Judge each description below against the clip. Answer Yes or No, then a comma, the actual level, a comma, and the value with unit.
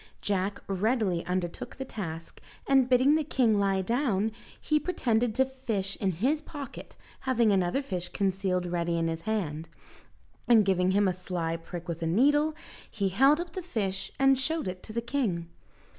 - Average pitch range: No, wide, 6.4 semitones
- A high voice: Yes, high, 205 Hz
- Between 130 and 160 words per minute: No, average, 175 wpm